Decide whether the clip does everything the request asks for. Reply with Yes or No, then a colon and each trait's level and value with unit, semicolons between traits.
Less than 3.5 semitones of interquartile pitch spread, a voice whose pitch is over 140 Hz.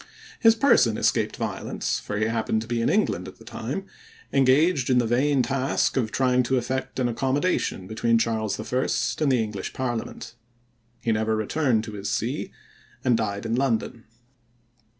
No: average, 3.1 semitones; low, 120 Hz